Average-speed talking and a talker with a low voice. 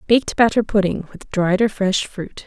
No: average, 195 wpm; high, 205 Hz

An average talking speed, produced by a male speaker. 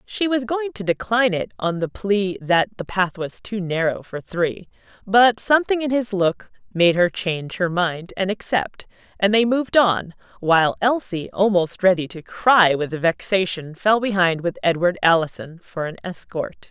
No: average, 175 wpm; female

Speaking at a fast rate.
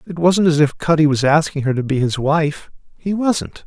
Yes: fast, 230 wpm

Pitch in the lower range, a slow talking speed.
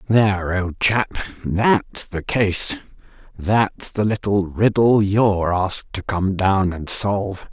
Yes: low, 100 Hz; slow, 130 wpm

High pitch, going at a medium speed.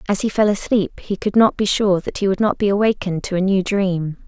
No: high, 195 Hz; fast, 265 wpm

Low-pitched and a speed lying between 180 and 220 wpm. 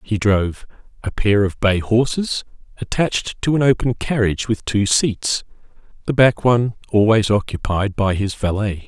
No: low, 110 Hz; average, 155 wpm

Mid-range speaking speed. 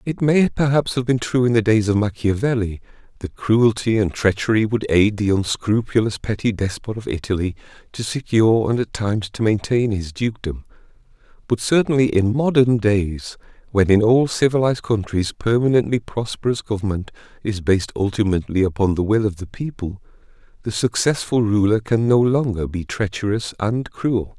Yes: average, 155 wpm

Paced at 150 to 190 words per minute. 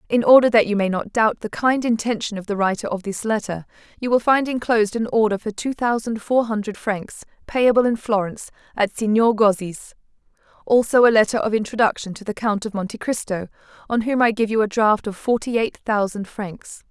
No: average, 200 wpm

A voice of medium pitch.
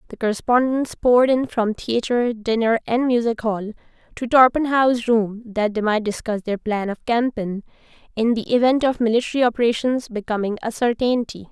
No: high, 230 Hz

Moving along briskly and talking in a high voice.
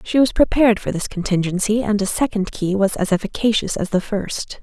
Yes: fast, 210 wpm; high, 205 Hz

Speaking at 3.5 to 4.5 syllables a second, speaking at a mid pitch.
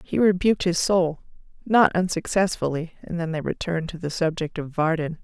No: 5.4 syllables/s; medium, 170 Hz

